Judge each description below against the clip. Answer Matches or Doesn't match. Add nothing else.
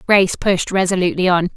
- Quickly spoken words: Doesn't match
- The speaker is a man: Doesn't match